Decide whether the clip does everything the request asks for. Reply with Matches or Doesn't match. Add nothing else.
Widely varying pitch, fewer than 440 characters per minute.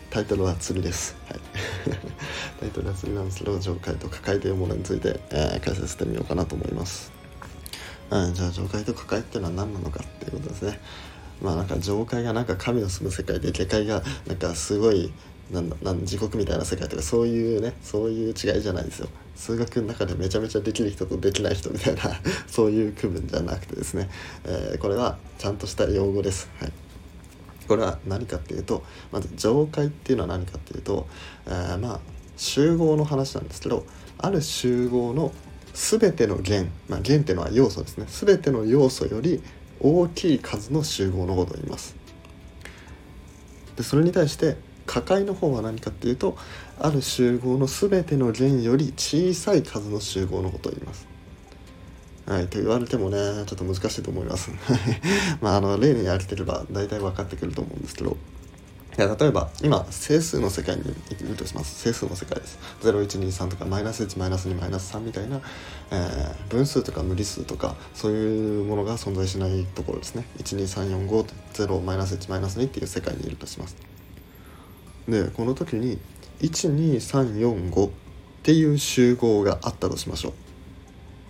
Doesn't match